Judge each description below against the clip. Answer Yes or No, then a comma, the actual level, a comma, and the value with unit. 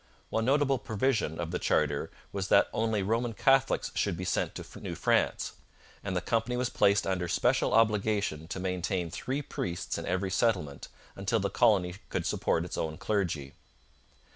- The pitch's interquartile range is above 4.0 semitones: Yes, average, 4.4 semitones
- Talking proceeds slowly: No, average, 165 wpm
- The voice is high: No, low, 100 Hz